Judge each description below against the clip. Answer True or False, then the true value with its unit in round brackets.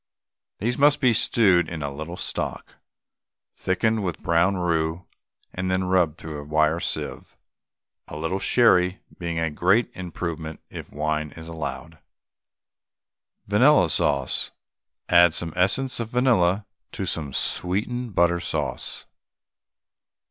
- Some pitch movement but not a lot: True (3.6 semitones)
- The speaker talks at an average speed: False (125 wpm)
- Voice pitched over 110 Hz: False (85 Hz)